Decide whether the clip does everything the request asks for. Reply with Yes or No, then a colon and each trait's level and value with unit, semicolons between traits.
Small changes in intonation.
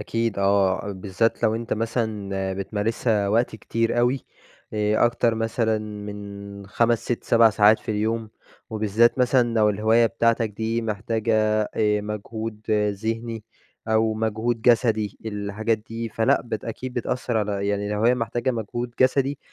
Yes: narrow, 1.8 semitones